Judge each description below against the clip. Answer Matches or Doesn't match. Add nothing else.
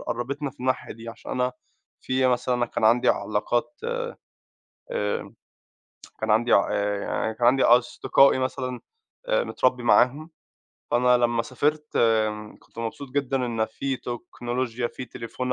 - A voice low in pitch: Matches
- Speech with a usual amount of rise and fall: Doesn't match